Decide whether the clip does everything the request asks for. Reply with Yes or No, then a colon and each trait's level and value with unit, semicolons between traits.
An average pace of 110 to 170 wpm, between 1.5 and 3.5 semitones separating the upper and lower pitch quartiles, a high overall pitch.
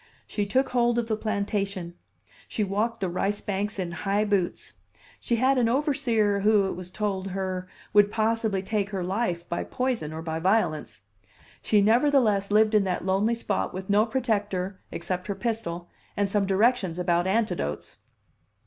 Yes: average, 165 wpm; average, 3.0 semitones; high, 205 Hz